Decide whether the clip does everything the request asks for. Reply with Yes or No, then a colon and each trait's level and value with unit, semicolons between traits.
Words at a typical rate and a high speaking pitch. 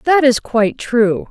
Yes: average, 185 wpm; high, 240 Hz